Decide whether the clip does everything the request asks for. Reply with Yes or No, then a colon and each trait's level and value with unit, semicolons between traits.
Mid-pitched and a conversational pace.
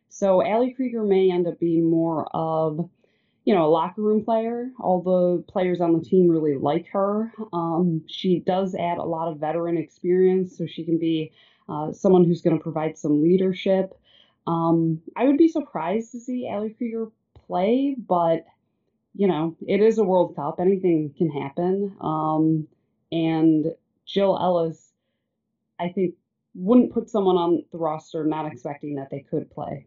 Yes: medium, 175 Hz; average, 170 wpm